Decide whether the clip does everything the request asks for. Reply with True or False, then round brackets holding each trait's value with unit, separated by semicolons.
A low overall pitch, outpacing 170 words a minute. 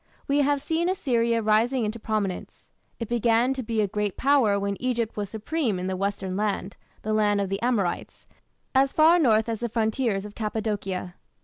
False (220 Hz; 185 wpm)